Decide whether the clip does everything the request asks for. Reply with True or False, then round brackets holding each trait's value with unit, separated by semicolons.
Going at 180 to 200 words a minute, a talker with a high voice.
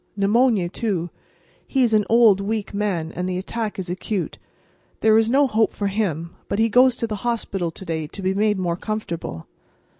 True (190 wpm; 205 Hz)